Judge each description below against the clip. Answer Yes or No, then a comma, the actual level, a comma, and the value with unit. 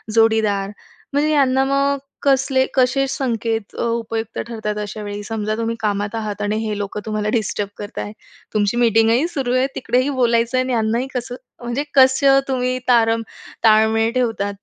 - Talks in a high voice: Yes, high, 230 Hz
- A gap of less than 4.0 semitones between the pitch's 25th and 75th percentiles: Yes, average, 3.1 semitones